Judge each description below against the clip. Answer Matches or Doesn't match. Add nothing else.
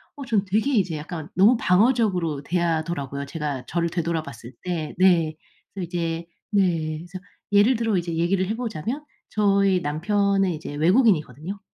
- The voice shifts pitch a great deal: Doesn't match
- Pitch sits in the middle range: Matches